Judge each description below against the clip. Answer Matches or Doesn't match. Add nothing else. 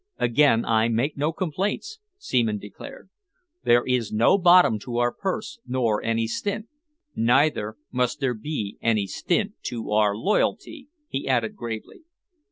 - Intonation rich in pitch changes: Matches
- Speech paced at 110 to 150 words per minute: Matches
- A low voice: Matches